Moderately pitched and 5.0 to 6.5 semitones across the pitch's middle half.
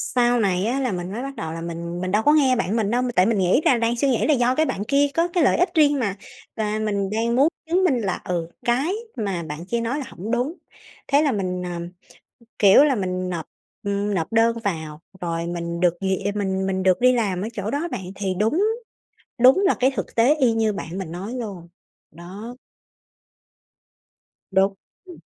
No: high, 210 Hz; wide, 5.6 semitones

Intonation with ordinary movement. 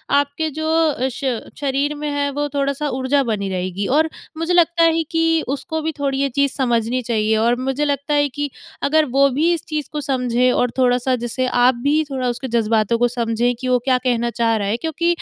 Yes: average, 3.6 semitones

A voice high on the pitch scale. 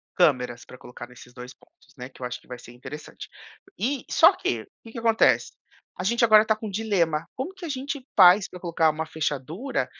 No: medium, 175 Hz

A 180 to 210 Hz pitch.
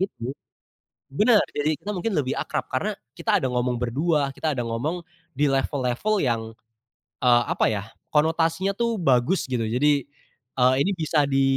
No: medium, 145 Hz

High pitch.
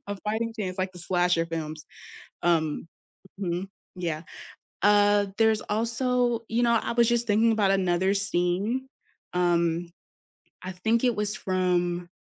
Yes: high, 195 Hz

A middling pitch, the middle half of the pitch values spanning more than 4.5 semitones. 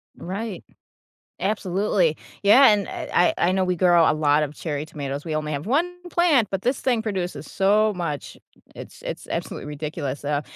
Yes: medium, 180 Hz; wide, 5.5 semitones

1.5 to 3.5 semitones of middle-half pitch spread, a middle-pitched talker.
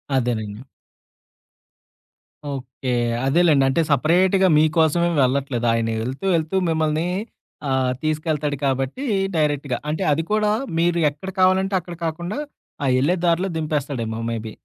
No: average, 4.4 semitones; medium, 155 Hz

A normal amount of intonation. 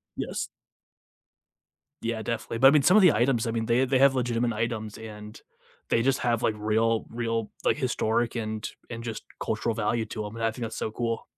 No: narrow, 1.5 semitones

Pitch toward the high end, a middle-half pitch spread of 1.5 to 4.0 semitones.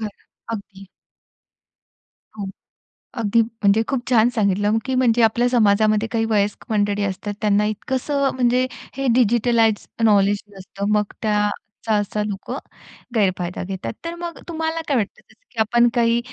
Yes: high, 220 Hz; average, 2.8 semitones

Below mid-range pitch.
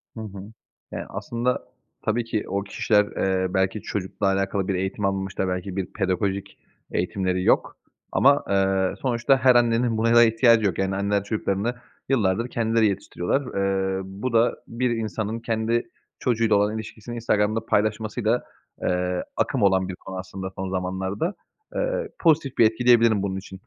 Yes: low, 105 Hz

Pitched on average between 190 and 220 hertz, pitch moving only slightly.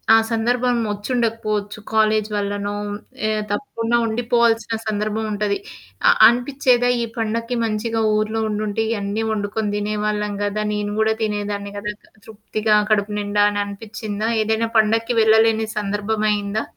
Yes: high, 215 Hz; narrow, 1.5 semitones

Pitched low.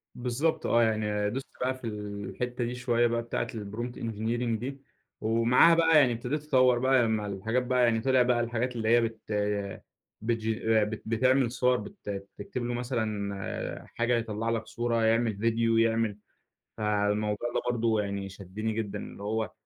Yes: low, 115 Hz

